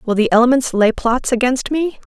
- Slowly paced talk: No, average, 200 wpm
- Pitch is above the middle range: Yes, high, 245 Hz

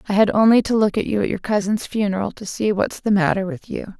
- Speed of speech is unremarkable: No, fast, 270 wpm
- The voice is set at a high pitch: Yes, high, 205 Hz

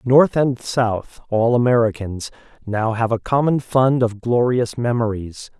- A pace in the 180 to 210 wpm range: No, average, 140 wpm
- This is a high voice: No, low, 120 Hz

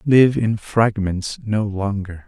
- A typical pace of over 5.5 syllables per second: No, 3.3 syllables/s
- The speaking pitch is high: No, low, 105 Hz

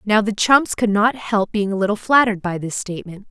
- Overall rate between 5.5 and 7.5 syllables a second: Yes, 5.6 syllables/s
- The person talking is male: No, female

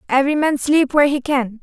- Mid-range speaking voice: No, very high, 280 Hz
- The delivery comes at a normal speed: No, fast, 220 wpm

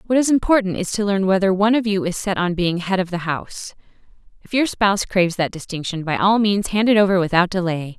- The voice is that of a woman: Yes, female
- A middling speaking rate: No, fast, 240 wpm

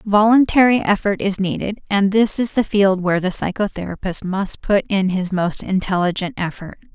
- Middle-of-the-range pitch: No, high, 195 Hz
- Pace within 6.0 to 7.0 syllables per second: No, 5.1 syllables/s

